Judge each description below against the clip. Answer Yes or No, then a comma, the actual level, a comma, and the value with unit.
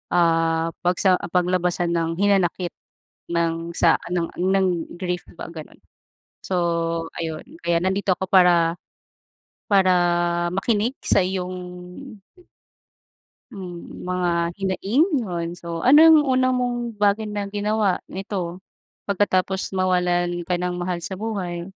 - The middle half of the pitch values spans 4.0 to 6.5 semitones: No, narrow, 2.6 semitones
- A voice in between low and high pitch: Yes, medium, 180 Hz